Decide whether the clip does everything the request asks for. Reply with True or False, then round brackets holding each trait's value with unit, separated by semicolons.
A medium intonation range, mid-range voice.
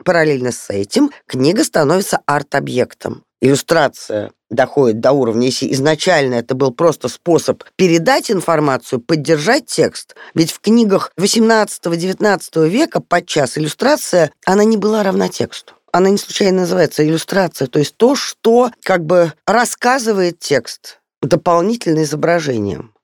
True (5.0 semitones; 175 Hz)